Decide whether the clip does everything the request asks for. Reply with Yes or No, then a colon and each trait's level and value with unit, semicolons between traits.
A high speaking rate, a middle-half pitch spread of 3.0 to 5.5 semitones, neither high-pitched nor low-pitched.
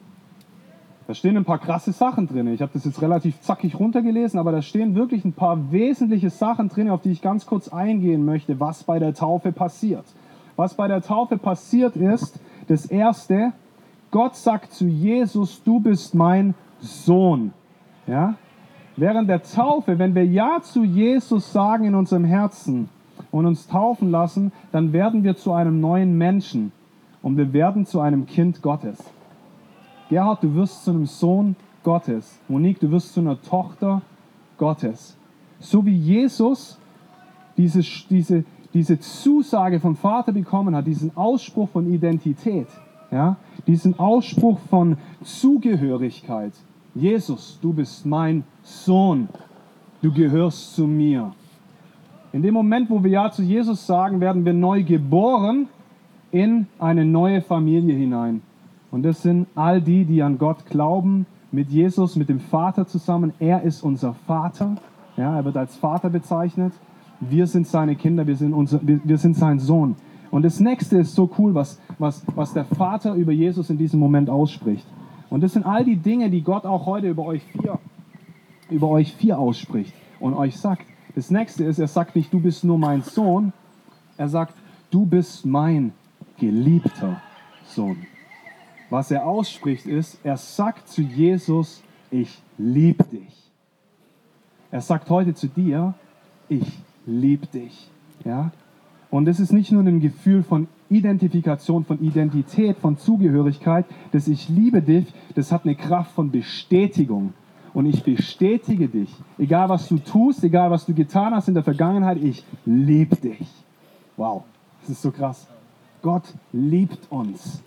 No: average, 155 wpm; average, 3.8 semitones; medium, 175 Hz